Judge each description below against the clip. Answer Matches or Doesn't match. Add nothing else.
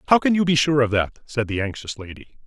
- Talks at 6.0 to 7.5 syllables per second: Matches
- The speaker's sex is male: Matches